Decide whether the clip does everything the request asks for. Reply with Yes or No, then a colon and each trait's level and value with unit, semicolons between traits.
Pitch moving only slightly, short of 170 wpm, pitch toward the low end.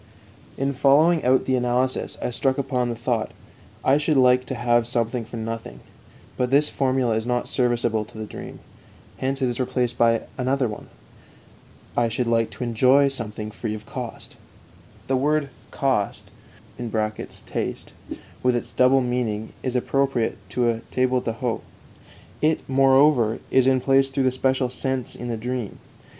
Yes: narrow, 2.2 semitones; average, 160 wpm; low, 125 Hz